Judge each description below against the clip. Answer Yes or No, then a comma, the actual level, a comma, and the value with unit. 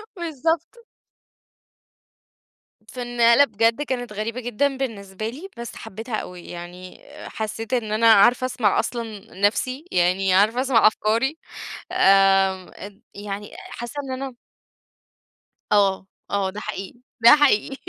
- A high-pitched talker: Yes, high, 225 Hz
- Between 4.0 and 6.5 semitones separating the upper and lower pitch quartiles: Yes, average, 4.3 semitones